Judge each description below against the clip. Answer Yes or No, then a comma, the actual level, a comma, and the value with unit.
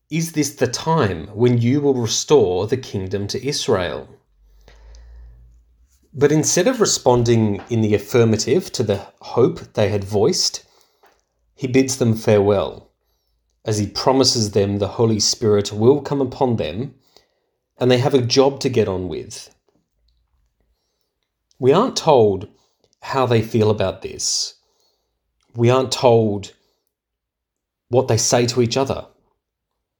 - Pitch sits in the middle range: No, low, 115 Hz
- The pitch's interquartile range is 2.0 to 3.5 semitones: No, average, 4.9 semitones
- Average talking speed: No, slow, 130 wpm